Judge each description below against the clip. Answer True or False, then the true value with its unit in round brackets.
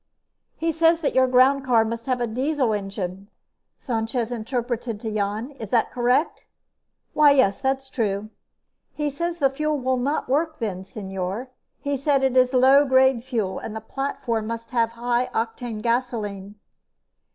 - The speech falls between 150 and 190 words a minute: True (155 wpm)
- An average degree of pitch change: True (3.5 semitones)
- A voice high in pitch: True (245 Hz)